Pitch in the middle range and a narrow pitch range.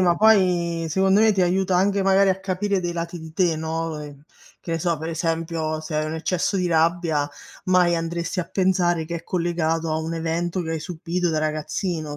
Yes: medium, 170 Hz; narrow, 2.2 semitones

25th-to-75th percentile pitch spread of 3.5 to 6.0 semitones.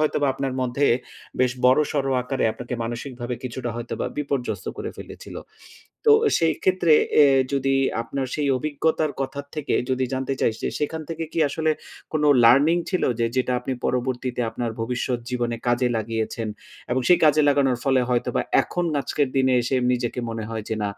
No: average, 3.0 semitones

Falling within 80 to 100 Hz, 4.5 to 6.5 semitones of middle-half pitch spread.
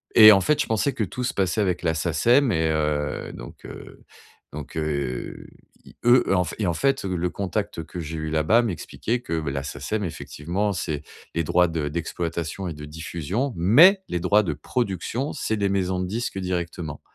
Yes: very low, 90 Hz; average, 5.0 semitones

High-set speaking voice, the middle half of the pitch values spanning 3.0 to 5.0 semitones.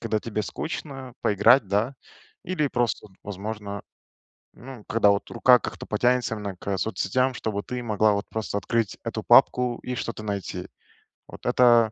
No: low, 110 Hz; average, 3.4 semitones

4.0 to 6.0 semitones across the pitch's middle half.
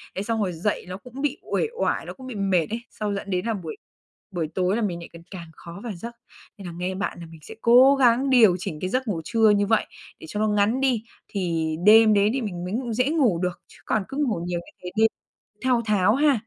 Yes: average, 4.7 semitones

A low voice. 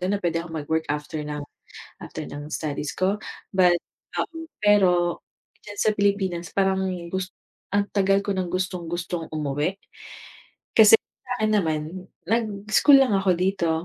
No: medium, 185 Hz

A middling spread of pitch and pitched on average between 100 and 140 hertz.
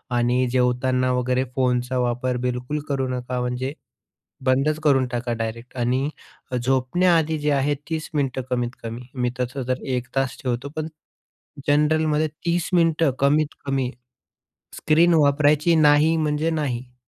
Yes: average, 3.3 semitones; low, 135 Hz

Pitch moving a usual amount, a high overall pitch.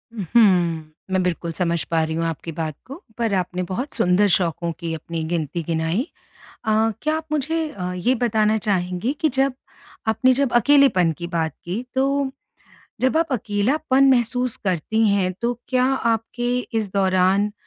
No: wide, 6.5 semitones; high, 205 Hz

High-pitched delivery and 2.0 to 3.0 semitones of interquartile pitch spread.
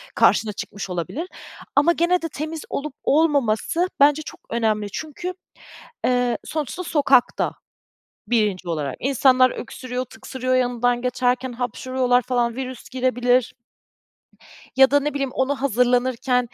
Yes: very high, 255 Hz; average, 2.7 semitones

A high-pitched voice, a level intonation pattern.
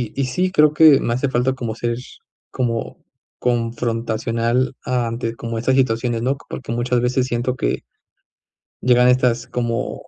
No: low, 125 Hz; narrow, 1.7 semitones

